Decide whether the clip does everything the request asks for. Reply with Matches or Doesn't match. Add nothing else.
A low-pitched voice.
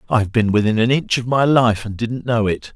Matches